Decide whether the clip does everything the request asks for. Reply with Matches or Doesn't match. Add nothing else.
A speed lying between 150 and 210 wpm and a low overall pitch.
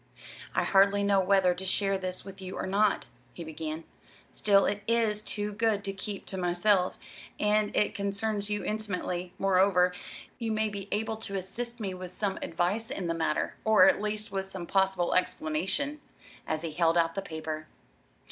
Doesn't match